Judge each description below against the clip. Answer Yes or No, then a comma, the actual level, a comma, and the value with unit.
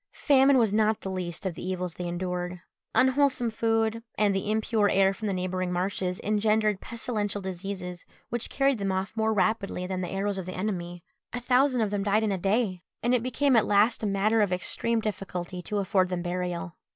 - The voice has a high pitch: Yes, high, 200 Hz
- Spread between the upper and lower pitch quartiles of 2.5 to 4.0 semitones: Yes, average, 3.3 semitones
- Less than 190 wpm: No, average, 200 wpm